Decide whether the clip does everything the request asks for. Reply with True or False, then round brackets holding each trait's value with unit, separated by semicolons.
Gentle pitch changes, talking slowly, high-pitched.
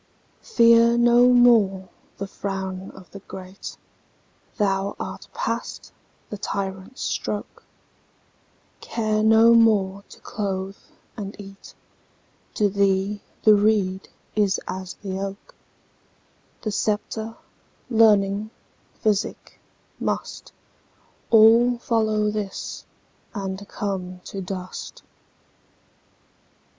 True (2.3 semitones; 80 wpm; 205 Hz)